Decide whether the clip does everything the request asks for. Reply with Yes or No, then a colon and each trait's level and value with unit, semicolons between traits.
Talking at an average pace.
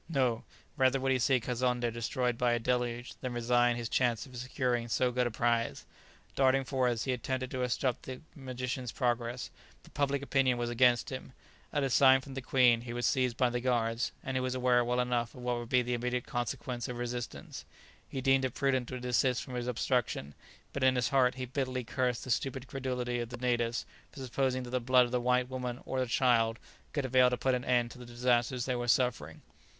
No: fast, 220 wpm